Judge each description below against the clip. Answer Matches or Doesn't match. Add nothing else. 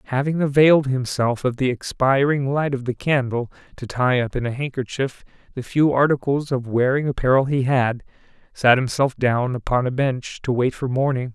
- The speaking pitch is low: Matches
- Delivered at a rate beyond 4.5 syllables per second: Matches